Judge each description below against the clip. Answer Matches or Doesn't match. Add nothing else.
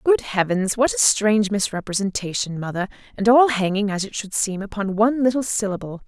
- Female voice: Matches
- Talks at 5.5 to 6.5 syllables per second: Matches